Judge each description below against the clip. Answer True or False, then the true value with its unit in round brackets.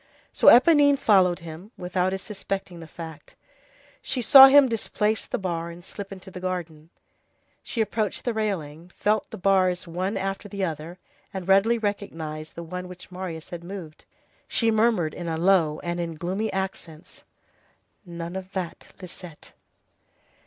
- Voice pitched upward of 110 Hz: True (185 Hz)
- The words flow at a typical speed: True (160 wpm)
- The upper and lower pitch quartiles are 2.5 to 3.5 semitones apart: True (3.1 semitones)